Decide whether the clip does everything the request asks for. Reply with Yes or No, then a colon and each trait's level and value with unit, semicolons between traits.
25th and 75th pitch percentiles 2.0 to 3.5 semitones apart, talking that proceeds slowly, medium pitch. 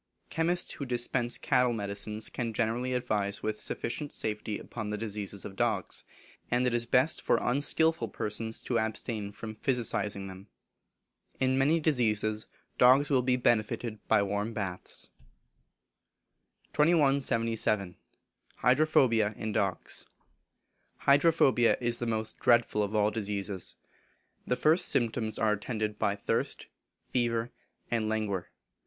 No: average, 3.0 semitones; slow, 125 wpm; low, 115 Hz